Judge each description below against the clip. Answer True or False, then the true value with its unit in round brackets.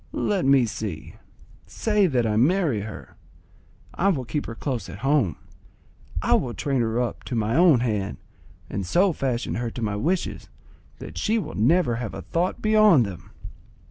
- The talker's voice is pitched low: True (125 Hz)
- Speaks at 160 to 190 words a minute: True (175 wpm)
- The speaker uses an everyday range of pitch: False (7.5 semitones)